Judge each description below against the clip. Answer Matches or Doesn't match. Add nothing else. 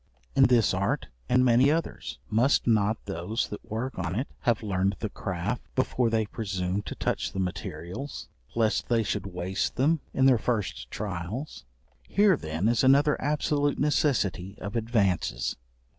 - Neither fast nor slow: Matches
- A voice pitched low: Matches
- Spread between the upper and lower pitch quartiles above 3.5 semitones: Matches